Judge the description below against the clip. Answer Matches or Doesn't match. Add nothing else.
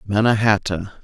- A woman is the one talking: Doesn't match